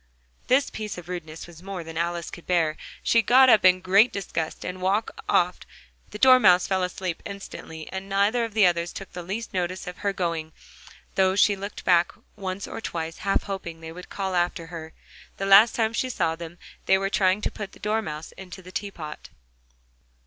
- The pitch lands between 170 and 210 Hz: Yes, medium, 185 Hz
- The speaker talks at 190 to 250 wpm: Yes, average, 200 wpm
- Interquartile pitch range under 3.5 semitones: Yes, average, 2.7 semitones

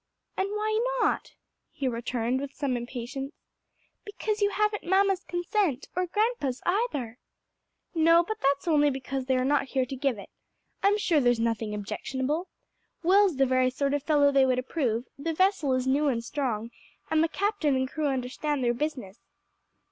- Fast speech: No, average, 170 wpm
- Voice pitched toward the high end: Yes, very high, 280 Hz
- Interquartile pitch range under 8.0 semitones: Yes, wide, 5.6 semitones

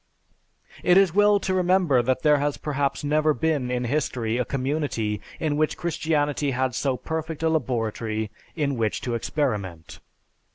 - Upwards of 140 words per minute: Yes, average, 155 wpm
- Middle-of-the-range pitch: Yes, medium, 145 Hz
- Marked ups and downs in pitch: No, average, 4.4 semitones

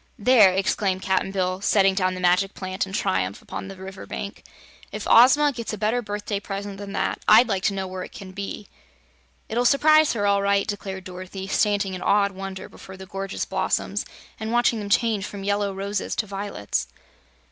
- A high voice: Yes, high, 200 Hz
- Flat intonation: Yes, narrow, 1.7 semitones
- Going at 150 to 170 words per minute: No, average, 190 wpm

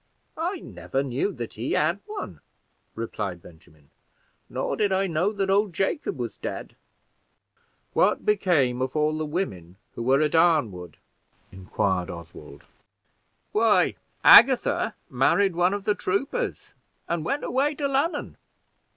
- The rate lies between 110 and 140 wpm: Yes, slow, 135 wpm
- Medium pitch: Yes, medium, 155 Hz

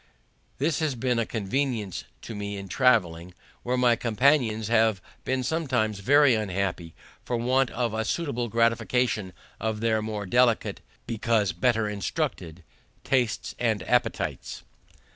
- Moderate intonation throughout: Yes, average, 3.2 semitones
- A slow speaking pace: Yes, slow, 130 wpm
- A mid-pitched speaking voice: No, low, 115 Hz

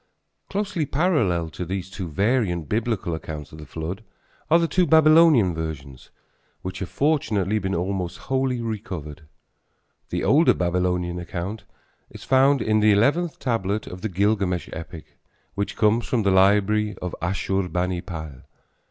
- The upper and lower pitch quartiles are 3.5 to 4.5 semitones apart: No, average, 5.0 semitones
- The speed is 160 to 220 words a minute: No, average, 140 wpm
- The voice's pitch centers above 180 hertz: No, very low, 95 Hz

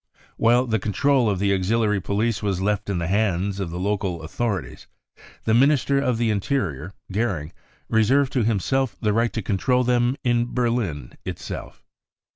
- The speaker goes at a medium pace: Yes, average, 160 wpm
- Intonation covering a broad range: No, average, 3.8 semitones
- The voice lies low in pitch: Yes, low, 110 Hz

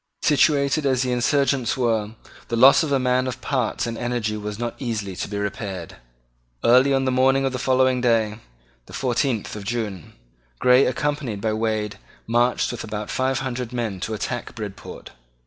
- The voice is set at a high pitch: No, low, 120 Hz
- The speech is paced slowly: No, average, 175 wpm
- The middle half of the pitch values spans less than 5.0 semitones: Yes, average, 3.3 semitones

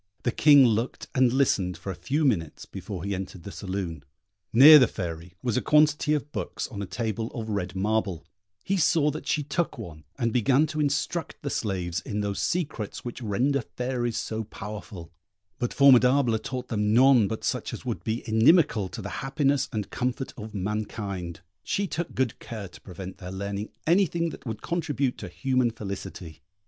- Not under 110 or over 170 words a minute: No, average, 180 wpm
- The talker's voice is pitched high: No, low, 115 Hz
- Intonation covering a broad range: Yes, wide, 5.7 semitones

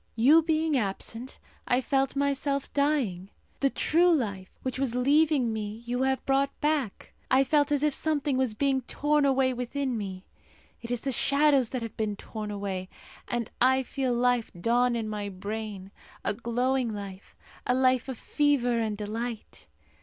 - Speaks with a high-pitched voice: Yes, very high, 250 Hz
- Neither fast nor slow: Yes, average, 165 wpm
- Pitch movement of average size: Yes, average, 4.1 semitones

